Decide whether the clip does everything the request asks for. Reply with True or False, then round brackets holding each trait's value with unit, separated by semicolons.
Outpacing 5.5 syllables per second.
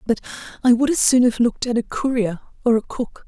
True (6.3 syllables/s)